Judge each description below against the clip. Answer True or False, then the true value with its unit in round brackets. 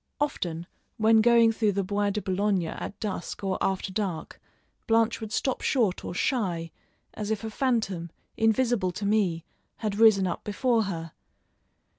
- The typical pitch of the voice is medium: False (205 Hz)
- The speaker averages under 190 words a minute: True (155 wpm)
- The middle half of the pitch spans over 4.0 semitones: False (3.2 semitones)